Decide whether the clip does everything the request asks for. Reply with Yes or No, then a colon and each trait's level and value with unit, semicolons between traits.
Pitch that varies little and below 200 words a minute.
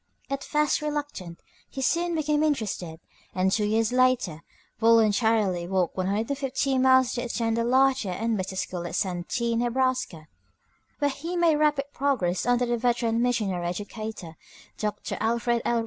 No: average, 5.3 semitones; average, 145 wpm